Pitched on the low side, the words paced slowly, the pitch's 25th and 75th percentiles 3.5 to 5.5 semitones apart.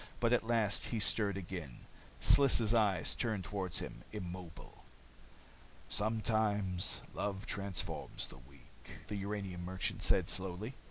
No: low, 100 Hz; slow, 120 wpm; average, 3.0 semitones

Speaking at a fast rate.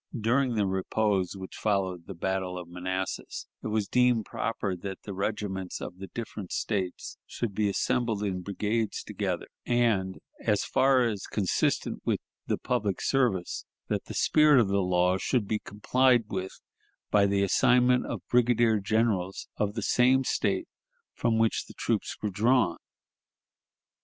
No: average, 150 wpm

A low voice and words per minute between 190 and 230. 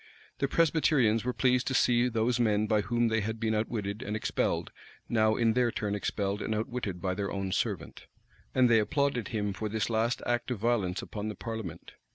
Yes: low, 110 Hz; average, 200 wpm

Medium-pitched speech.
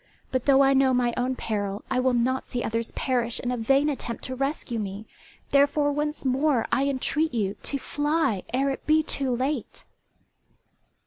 No: very high, 260 Hz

